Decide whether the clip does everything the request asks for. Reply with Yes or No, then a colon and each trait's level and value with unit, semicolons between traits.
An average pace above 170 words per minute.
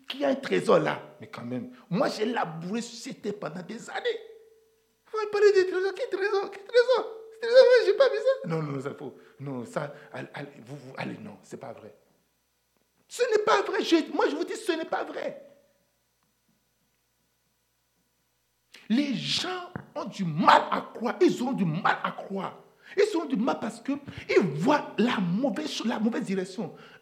Yes: average, 185 wpm